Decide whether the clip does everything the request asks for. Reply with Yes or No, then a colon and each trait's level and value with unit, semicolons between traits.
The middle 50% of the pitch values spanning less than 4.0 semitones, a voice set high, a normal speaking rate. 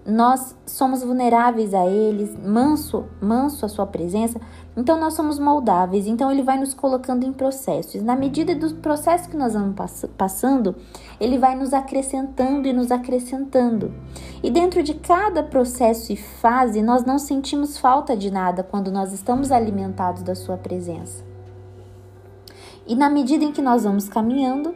No: average, 5.2 semitones; very high, 250 Hz; average, 160 wpm